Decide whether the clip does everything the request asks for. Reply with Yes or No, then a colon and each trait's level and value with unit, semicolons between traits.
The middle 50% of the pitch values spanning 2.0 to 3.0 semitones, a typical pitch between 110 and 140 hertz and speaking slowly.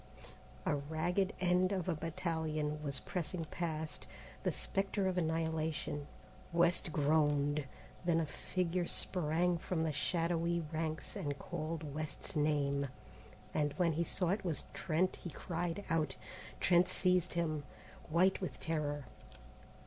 No: average, 2.7 semitones; medium, 165 Hz; slow, 130 wpm